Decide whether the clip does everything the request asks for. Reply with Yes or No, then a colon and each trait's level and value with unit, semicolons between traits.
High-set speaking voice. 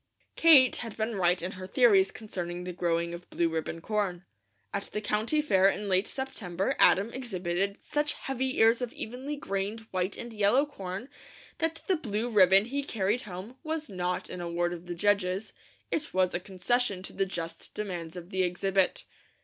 Yes: high, 195 Hz